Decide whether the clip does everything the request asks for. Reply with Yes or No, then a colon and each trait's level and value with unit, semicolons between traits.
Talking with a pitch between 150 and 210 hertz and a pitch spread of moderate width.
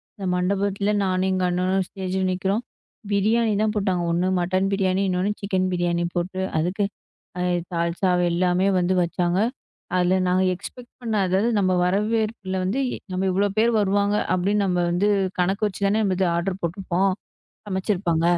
No: high, 190 Hz; narrow, 1.9 semitones